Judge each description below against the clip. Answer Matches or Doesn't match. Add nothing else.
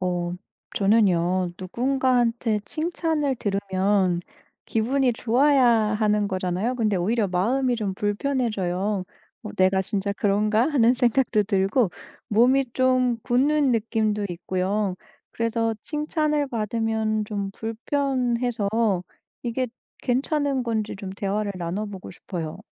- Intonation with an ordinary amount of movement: Matches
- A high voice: Matches